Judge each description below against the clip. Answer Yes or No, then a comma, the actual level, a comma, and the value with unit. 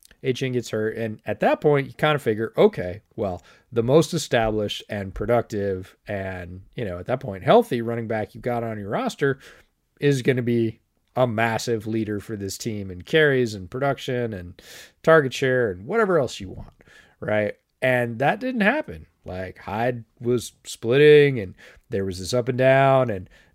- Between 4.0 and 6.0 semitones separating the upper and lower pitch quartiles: Yes, average, 4.3 semitones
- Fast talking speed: No, average, 180 wpm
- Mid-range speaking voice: No, low, 115 Hz